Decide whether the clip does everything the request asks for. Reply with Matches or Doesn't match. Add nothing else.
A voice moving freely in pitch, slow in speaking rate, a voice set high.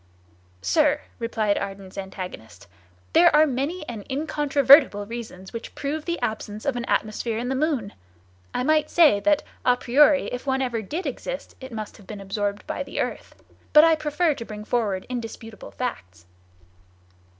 Doesn't match